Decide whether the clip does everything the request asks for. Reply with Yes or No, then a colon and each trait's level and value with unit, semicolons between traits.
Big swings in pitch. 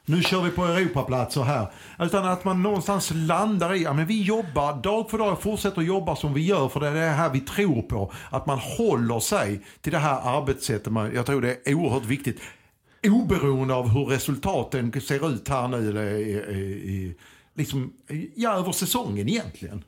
Yes: wide, 6.8 semitones